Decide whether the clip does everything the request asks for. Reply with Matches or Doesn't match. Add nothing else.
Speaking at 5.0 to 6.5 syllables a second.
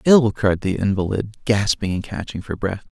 Doesn't match